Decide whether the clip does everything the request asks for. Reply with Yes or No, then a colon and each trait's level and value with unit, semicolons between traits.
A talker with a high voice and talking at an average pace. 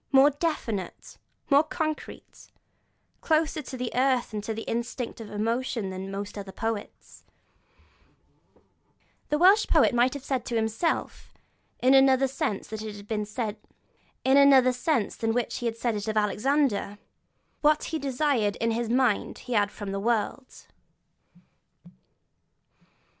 No: high, 240 Hz; slow, 120 wpm